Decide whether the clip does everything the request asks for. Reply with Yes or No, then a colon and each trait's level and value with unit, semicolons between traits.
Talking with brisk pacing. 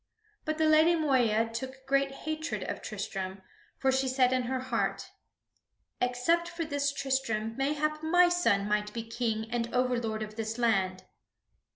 No: average, 155 wpm